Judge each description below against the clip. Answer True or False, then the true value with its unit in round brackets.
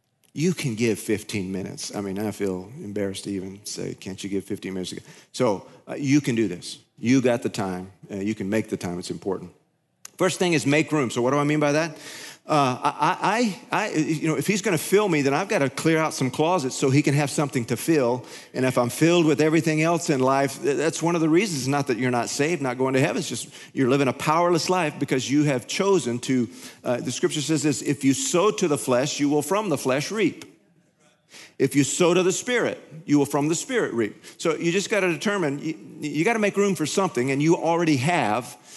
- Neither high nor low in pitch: True (145 Hz)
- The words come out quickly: True (235 wpm)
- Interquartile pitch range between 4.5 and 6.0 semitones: True (4.8 semitones)